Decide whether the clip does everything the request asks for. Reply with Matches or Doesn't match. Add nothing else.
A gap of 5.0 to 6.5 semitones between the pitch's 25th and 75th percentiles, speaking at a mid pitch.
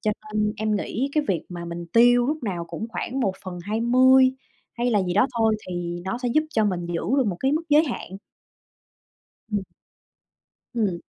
Doesn't match